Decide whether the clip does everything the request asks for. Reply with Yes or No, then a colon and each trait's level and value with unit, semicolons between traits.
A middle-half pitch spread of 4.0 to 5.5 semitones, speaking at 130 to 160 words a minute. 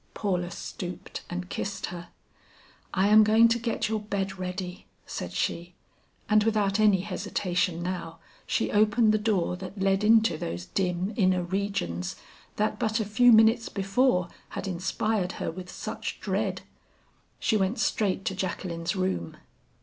No: average, 3.1 semitones; average, 150 wpm